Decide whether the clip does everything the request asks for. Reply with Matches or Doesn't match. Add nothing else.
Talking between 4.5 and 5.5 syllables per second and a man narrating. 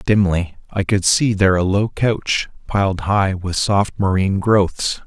Doesn't match